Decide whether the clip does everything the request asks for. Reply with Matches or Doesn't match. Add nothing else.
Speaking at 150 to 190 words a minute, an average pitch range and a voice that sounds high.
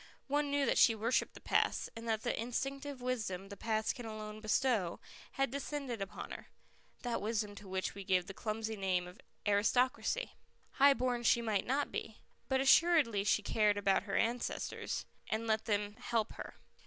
Matches